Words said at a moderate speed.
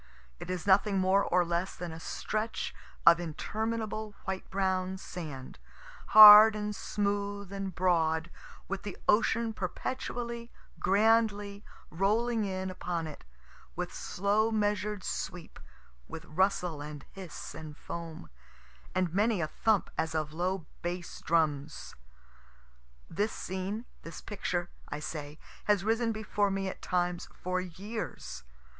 No: slow, 125 wpm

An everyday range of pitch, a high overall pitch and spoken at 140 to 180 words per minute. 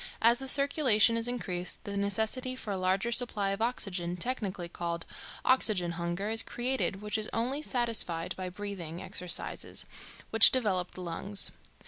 Yes: average, 4.7 semitones; high, 205 Hz; average, 150 wpm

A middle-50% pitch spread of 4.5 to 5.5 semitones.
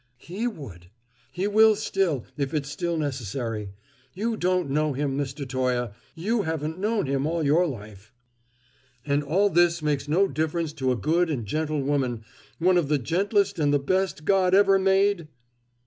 Yes: average, 5.2 semitones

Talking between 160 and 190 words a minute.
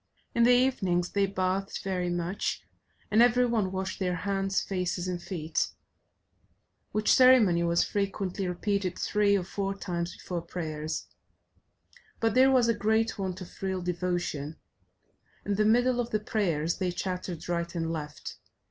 No: average, 150 wpm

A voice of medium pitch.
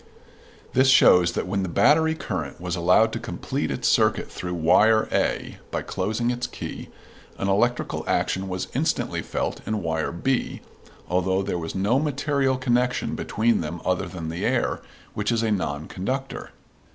No: low, 100 Hz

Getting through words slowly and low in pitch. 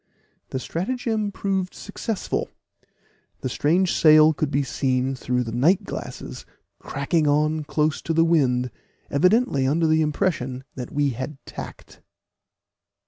No: slow, 130 wpm; medium, 150 Hz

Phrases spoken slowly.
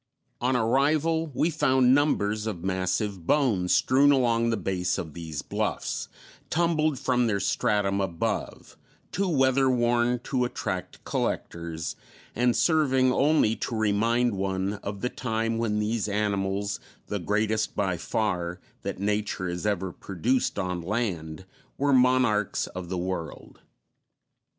Yes: slow, 130 wpm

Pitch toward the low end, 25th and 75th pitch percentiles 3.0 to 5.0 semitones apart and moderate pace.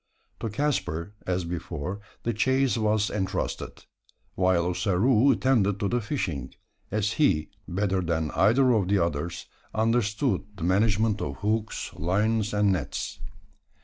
No: low, 100 Hz; average, 3.7 semitones; slow, 130 wpm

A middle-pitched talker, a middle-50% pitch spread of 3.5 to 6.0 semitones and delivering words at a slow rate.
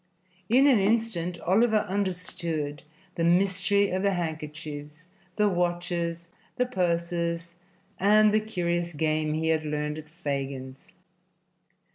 Yes: medium, 170 Hz; average, 3.9 semitones; slow, 115 wpm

